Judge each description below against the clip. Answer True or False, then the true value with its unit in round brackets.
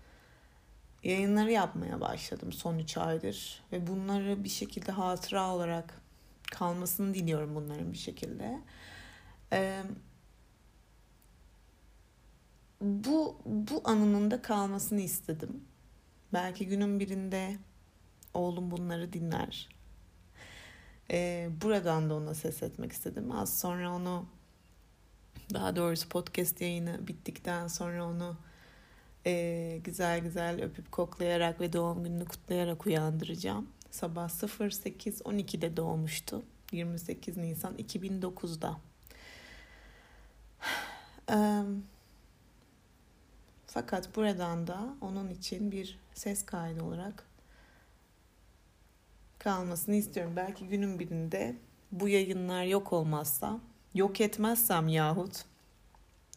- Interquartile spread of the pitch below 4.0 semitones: True (3.4 semitones)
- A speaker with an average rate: False (90 wpm)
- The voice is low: False (175 Hz)